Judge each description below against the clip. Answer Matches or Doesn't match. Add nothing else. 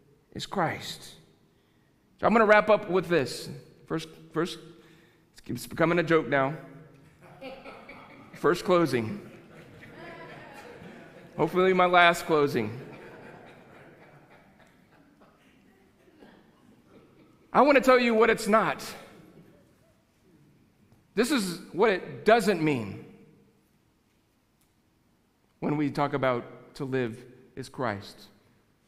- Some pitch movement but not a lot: Doesn't match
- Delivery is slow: Matches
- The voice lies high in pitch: Doesn't match